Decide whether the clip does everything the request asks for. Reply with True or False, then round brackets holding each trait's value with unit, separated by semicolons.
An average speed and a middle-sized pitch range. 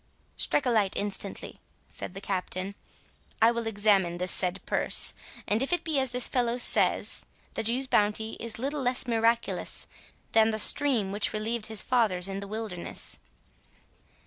True (160 wpm; 3.3 semitones)